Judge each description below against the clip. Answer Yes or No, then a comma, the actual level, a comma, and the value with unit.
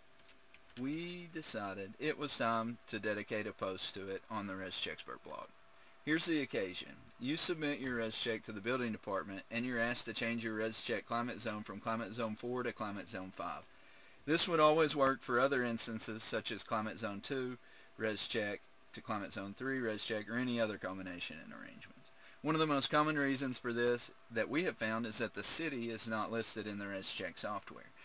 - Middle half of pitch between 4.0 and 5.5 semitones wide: No, average, 3.5 semitones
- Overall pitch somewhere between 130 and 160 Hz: No, low, 115 Hz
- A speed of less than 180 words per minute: No, average, 195 wpm